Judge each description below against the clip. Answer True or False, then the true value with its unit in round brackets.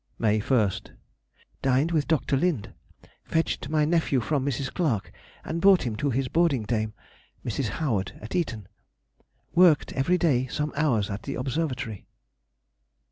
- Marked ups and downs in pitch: True (6.0 semitones)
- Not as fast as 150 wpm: True (135 wpm)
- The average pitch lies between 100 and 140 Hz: True (135 Hz)